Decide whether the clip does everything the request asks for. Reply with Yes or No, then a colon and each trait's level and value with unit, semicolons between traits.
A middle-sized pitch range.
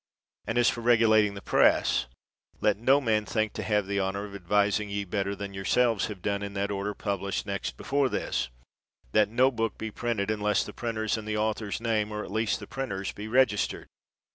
No: narrow, 2.1 semitones